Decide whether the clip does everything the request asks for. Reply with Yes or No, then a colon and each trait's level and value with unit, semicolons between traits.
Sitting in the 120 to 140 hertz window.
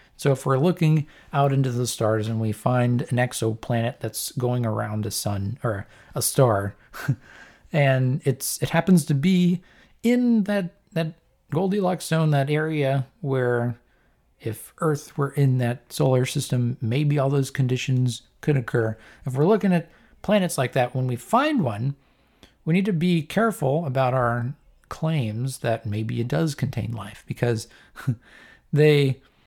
Yes: low, 135 Hz